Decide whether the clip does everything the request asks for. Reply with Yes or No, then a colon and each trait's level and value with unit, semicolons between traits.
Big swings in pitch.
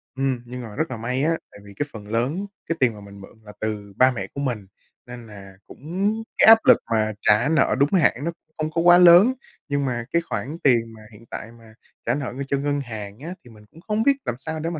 Yes: wide, 6.2 semitones